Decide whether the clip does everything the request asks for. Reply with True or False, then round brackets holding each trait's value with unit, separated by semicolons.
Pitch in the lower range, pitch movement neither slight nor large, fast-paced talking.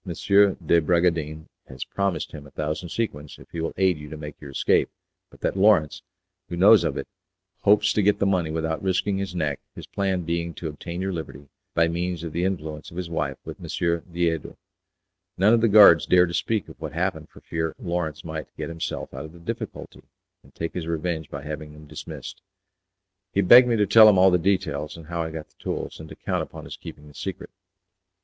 True (85 Hz; 3.5 semitones; 215 wpm)